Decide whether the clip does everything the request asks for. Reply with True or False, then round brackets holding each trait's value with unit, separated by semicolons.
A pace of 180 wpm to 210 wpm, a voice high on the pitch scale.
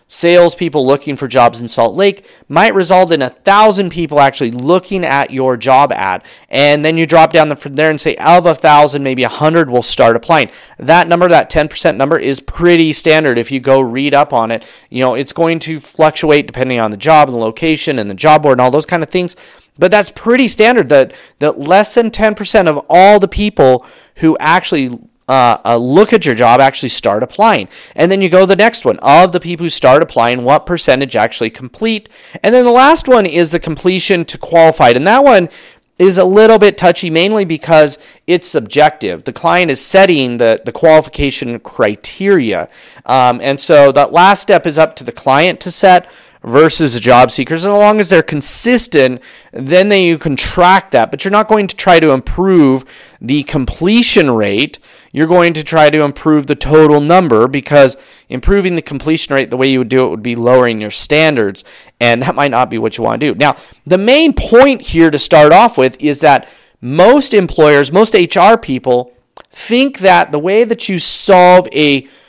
False (205 wpm; 155 Hz)